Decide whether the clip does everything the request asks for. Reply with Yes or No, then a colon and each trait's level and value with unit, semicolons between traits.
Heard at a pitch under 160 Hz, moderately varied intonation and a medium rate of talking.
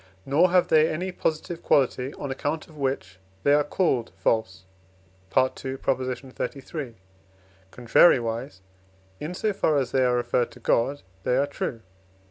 Yes: low, 135 Hz; average, 4.0 semitones; average, 145 wpm